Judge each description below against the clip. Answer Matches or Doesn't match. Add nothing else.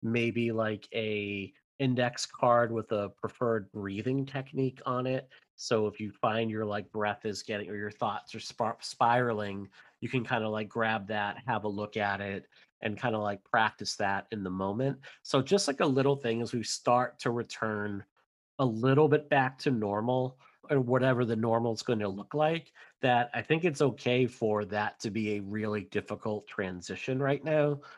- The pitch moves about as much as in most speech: Matches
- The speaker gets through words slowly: Doesn't match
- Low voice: Matches